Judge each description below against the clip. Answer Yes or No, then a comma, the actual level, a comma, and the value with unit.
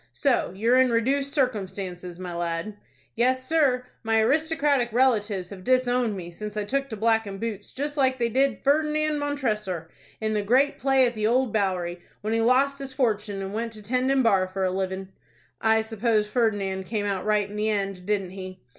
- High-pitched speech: Yes, high, 220 Hz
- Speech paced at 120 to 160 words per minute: No, average, 190 wpm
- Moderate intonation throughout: Yes, average, 4.8 semitones